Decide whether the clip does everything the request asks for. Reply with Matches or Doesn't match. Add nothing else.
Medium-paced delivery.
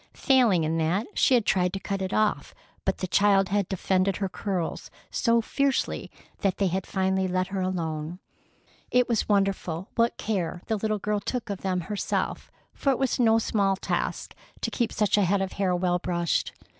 Matches